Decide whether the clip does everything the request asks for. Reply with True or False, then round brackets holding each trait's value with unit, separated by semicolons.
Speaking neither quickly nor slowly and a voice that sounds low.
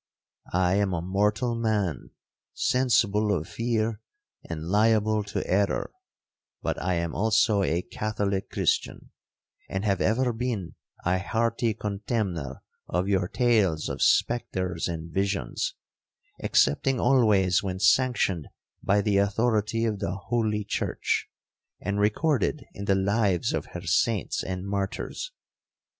False (120 wpm; 100 Hz)